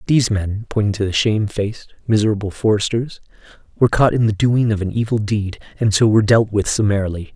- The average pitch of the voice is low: Yes, low, 105 Hz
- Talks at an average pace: Yes, average, 190 wpm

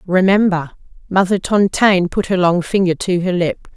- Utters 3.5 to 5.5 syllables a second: Yes, 4.9 syllables/s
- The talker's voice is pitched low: No, medium, 185 Hz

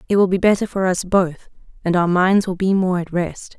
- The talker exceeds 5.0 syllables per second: Yes, 5.2 syllables/s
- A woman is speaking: Yes, female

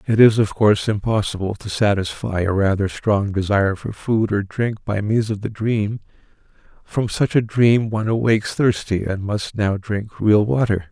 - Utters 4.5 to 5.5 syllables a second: Yes, 4.7 syllables/s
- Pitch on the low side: Yes, low, 105 Hz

